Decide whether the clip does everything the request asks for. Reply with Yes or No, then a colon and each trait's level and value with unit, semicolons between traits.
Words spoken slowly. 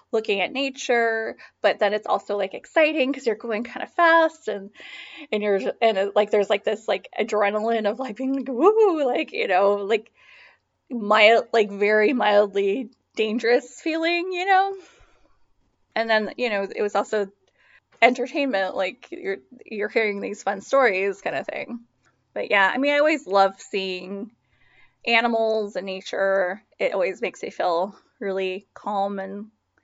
No: average, 160 wpm